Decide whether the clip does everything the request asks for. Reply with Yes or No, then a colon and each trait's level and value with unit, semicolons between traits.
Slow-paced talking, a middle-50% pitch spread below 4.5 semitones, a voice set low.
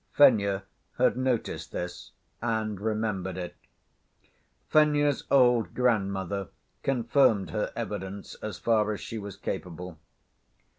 Yes: slow, 105 wpm; average, 3.8 semitones; low, 105 Hz